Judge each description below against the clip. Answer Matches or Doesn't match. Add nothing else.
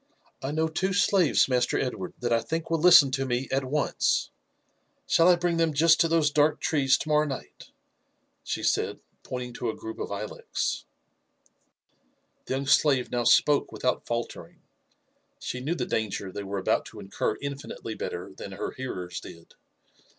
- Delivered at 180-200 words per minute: Doesn't match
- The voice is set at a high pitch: Doesn't match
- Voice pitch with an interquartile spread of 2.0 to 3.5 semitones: Doesn't match